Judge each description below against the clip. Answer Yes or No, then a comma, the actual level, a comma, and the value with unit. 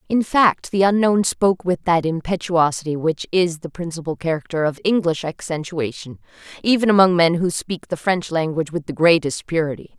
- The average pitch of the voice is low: No, medium, 170 Hz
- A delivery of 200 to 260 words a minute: No, average, 170 wpm